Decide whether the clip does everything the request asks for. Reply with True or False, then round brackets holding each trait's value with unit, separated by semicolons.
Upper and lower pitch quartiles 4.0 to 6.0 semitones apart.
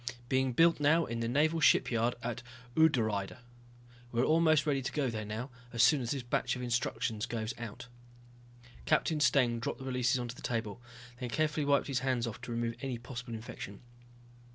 False (3.4 semitones)